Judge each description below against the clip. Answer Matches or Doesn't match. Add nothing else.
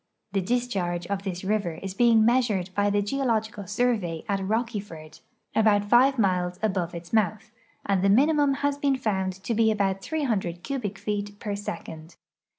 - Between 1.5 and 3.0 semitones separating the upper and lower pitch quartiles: Doesn't match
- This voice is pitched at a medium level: Doesn't match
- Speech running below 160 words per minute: Doesn't match